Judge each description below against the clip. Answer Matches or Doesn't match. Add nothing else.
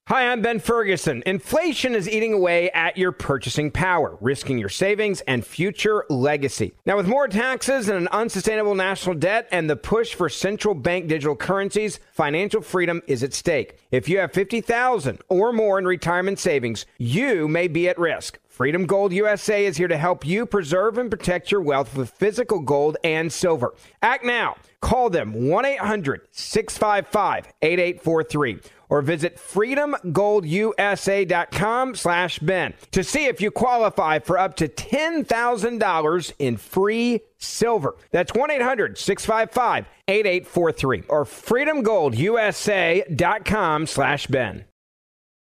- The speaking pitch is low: Doesn't match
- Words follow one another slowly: Matches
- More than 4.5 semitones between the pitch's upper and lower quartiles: Matches